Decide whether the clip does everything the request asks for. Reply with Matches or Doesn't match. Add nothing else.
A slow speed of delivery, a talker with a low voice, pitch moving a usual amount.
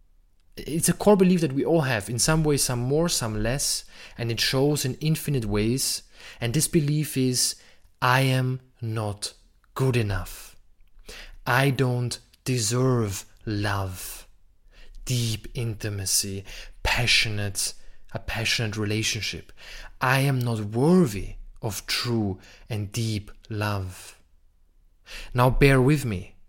Matches